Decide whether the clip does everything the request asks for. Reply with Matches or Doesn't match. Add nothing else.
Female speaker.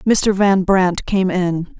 Matches